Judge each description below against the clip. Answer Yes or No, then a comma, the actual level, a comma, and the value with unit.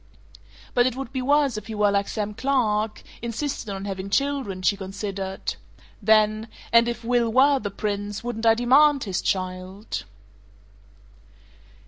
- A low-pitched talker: No, high, 220 Hz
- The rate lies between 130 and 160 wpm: Yes, average, 140 wpm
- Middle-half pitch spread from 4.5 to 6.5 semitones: No, average, 3.7 semitones